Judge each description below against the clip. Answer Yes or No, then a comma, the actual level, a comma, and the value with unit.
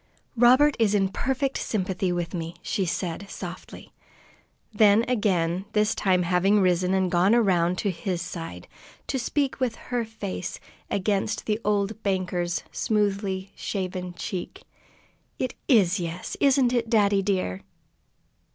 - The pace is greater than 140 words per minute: No, slow, 135 wpm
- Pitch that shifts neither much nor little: Yes, average, 3.5 semitones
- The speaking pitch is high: Yes, high, 195 Hz